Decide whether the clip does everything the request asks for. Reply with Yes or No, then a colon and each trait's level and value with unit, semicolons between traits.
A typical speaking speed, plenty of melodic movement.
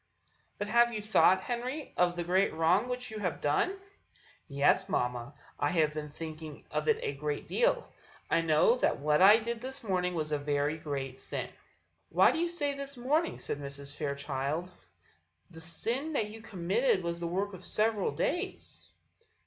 Yes: average, 175 wpm; wide, 7.9 semitones